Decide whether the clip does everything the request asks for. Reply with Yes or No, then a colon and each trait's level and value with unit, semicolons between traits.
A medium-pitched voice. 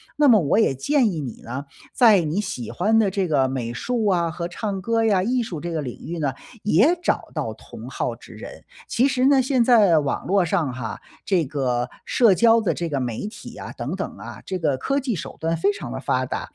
Yes: medium, 180 Hz